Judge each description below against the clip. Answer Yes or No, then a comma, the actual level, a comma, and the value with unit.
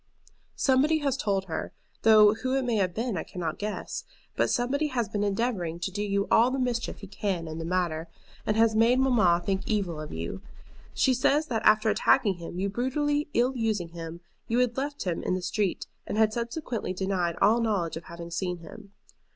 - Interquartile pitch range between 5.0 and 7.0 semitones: Yes, average, 5.3 semitones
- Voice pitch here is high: Yes, high, 210 Hz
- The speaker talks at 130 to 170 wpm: No, average, 200 wpm